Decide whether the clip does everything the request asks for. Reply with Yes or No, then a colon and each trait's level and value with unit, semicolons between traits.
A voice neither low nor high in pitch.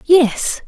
No: very high, 300 Hz